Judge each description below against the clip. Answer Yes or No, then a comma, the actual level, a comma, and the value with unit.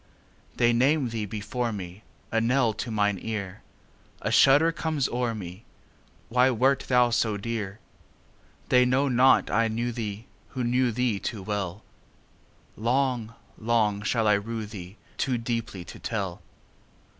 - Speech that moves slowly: Yes, slow, 120 wpm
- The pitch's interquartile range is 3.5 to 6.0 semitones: No, average, 3.1 semitones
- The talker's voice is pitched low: Yes, low, 115 Hz